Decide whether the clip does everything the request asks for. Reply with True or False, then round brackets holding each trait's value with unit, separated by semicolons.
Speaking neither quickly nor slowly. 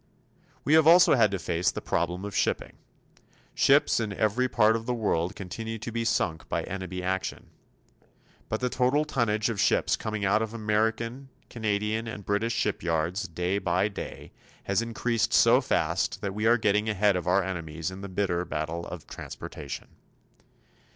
True (170 wpm)